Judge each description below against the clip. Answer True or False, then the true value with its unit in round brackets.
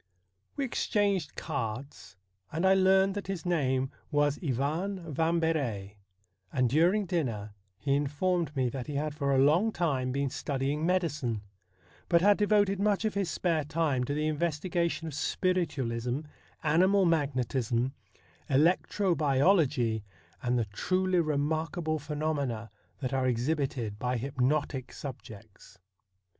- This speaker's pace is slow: True (130 wpm)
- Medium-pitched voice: True (150 Hz)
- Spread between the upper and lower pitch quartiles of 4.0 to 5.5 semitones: True (5.0 semitones)